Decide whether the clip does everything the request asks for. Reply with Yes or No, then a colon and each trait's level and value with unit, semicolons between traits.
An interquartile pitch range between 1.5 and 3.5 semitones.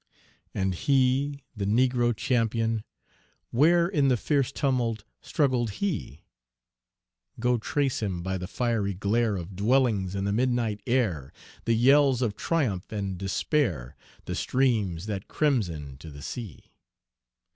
No: average, 5.0 semitones